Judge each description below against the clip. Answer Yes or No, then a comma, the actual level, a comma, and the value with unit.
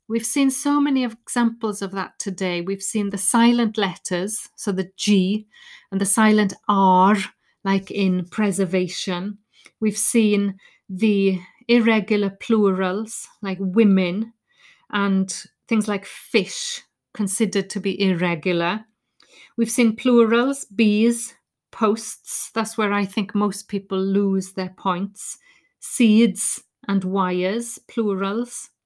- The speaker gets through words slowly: Yes, slow, 115 wpm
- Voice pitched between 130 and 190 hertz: No, high, 205 Hz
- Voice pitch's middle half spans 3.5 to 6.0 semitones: No, average, 3.0 semitones